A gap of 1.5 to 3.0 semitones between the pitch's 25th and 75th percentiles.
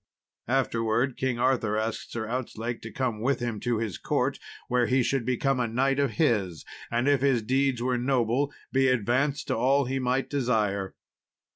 Yes: average, 2.7 semitones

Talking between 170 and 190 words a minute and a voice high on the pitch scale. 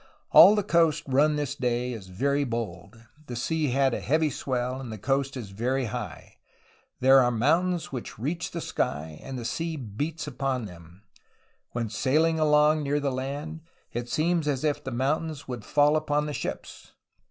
No: average, 175 wpm; low, 135 Hz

